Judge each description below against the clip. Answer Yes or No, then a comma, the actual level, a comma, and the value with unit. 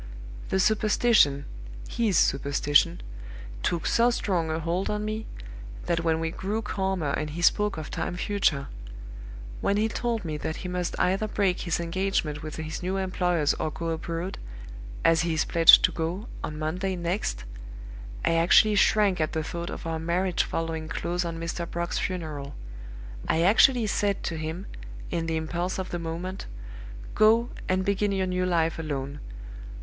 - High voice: No, medium, 175 Hz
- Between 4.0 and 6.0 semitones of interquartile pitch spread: No, average, 3.1 semitones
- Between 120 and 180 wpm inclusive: Yes, average, 165 wpm